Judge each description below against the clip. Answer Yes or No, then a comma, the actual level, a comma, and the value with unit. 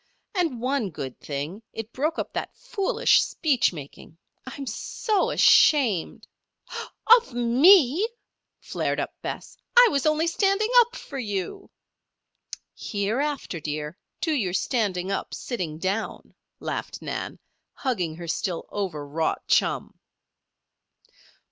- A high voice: Yes, high, 235 Hz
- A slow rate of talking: Yes, slow, 115 wpm